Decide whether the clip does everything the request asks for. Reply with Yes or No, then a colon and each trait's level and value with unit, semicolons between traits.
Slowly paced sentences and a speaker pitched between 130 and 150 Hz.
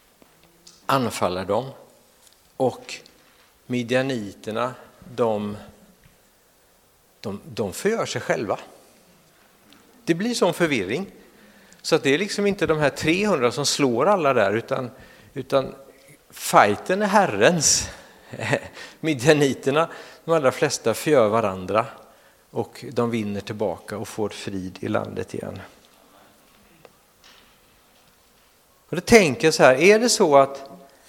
Yes: slow, 110 wpm; low, 135 Hz